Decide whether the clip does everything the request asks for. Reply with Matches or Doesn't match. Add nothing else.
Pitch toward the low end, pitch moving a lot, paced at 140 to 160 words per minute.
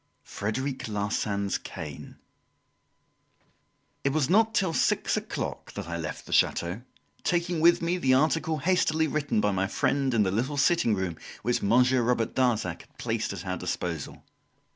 Matches